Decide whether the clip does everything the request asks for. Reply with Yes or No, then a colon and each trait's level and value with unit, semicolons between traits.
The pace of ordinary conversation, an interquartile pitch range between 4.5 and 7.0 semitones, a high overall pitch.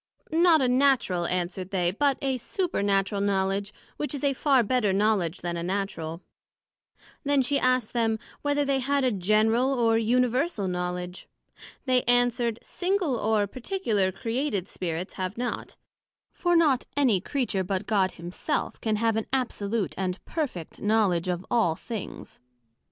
Yes: average, 145 wpm; wide, 5.5 semitones; high, 220 Hz